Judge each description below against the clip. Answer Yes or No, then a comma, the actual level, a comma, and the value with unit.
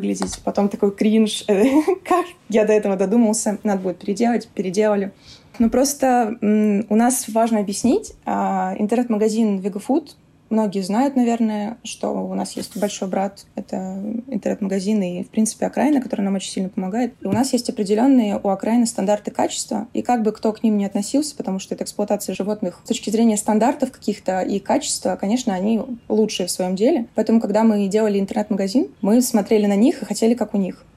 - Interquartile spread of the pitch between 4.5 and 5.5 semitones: No, average, 2.8 semitones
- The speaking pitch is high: Yes, high, 215 Hz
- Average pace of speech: No, fast, 180 wpm